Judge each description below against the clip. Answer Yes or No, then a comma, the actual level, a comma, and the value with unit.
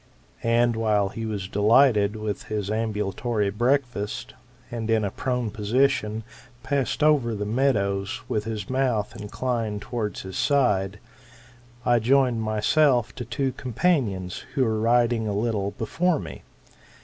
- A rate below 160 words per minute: Yes, slow, 135 wpm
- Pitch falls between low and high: No, low, 110 Hz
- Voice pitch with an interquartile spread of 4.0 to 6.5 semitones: No, average, 3.3 semitones